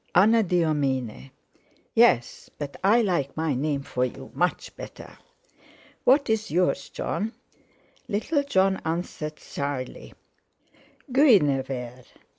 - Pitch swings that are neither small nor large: No, wide, 7.4 semitones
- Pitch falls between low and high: Yes, medium, 160 Hz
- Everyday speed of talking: No, slow, 95 wpm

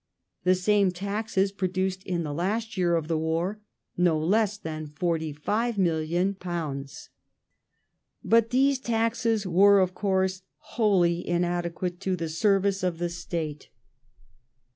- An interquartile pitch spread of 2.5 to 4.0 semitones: Yes, average, 3.0 semitones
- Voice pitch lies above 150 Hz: Yes, medium, 185 Hz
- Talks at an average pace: No, slow, 115 wpm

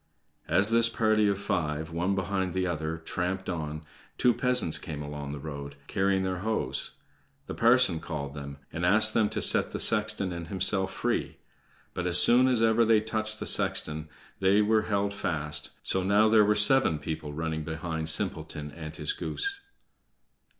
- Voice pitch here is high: No, very low, 95 Hz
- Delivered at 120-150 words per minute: No, average, 170 wpm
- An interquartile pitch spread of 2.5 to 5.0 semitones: No, wide, 5.4 semitones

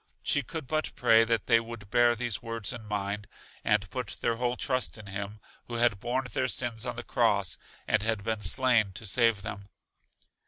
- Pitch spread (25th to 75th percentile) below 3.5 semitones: Yes, narrow, 2.6 semitones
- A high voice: No, low, 115 Hz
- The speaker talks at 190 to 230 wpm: Yes, average, 195 wpm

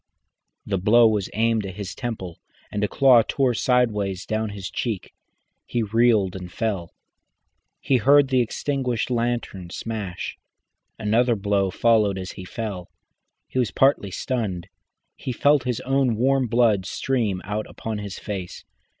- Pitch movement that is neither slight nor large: Yes, average, 3.8 semitones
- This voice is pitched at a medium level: No, low, 110 Hz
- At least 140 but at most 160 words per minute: Yes, average, 150 wpm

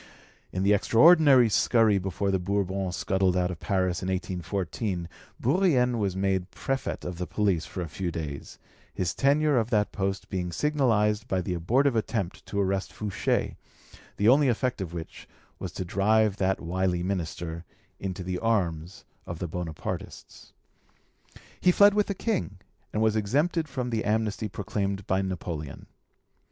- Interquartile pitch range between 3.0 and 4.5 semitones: Yes, average, 3.9 semitones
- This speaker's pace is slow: No, average, 155 wpm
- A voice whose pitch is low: Yes, low, 100 Hz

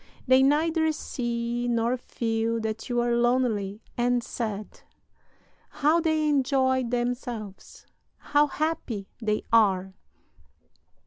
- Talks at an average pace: No, slow, 105 wpm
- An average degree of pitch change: Yes, average, 3.2 semitones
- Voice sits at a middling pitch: No, high, 240 Hz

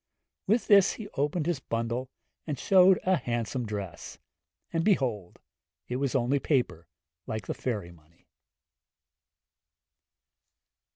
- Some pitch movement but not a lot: No, wide, 7.2 semitones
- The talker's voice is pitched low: Yes, low, 130 Hz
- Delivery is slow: Yes, slow, 115 wpm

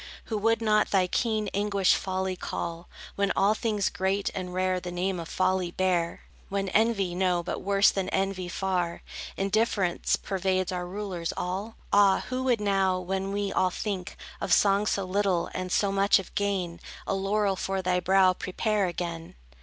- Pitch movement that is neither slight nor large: No, narrow, 1.8 semitones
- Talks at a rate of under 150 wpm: No, average, 170 wpm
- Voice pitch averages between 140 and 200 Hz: Yes, high, 190 Hz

